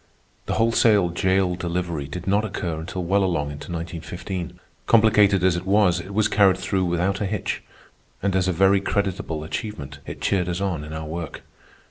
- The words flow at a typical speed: Yes, average, 180 wpm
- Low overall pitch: Yes, very low, 90 Hz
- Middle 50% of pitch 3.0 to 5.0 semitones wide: No, narrow, 2.6 semitones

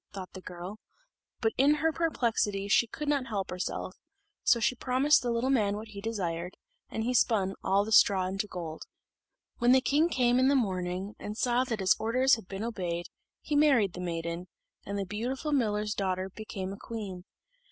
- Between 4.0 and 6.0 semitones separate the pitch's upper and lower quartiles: Yes, average, 4.9 semitones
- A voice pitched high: Yes, high, 210 Hz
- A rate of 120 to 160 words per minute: No, average, 190 wpm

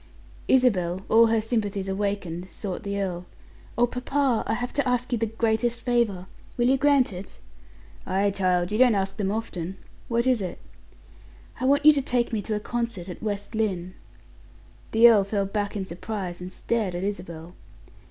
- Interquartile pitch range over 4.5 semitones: No, average, 3.9 semitones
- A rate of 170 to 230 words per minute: Yes, average, 180 wpm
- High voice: Yes, high, 210 Hz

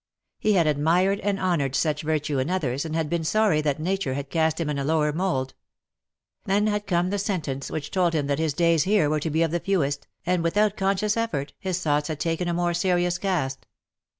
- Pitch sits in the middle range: Yes, medium, 165 Hz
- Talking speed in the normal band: No, fast, 220 wpm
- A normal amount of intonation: Yes, average, 4.0 semitones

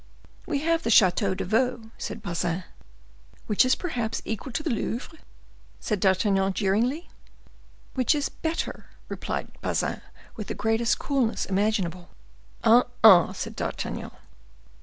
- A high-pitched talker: Yes, high, 225 Hz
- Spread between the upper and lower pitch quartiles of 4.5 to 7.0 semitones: Yes, average, 4.8 semitones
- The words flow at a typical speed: No, slow, 130 wpm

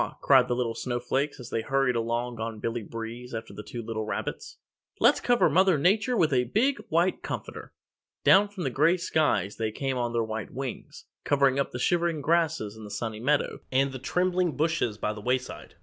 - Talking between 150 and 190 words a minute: No, average, 200 wpm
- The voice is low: Yes, low, 130 Hz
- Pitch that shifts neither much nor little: No, wide, 6.0 semitones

